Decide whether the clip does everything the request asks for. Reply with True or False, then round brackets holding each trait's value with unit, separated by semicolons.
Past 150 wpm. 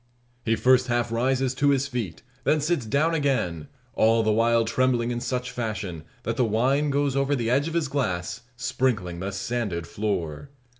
True (180 wpm)